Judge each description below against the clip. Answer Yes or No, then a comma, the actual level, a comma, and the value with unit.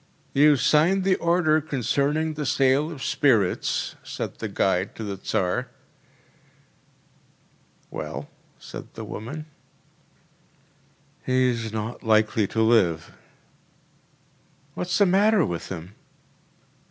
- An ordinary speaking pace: No, slow, 105 wpm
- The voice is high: No, low, 130 Hz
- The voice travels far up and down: Yes, wide, 6.4 semitones